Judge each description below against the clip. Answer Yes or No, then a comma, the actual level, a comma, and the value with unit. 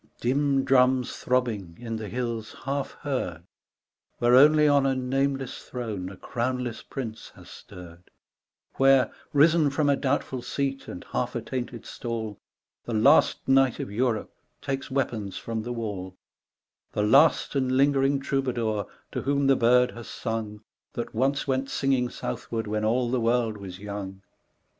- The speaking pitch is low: Yes, low, 125 Hz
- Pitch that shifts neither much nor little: Yes, average, 3.6 semitones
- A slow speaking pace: No, average, 150 wpm